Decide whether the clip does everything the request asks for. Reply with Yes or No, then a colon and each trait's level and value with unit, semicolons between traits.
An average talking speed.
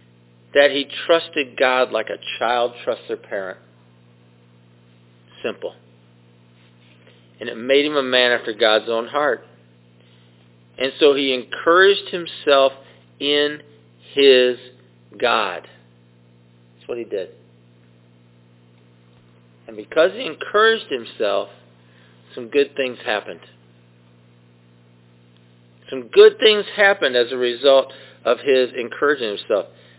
No: slow, 105 wpm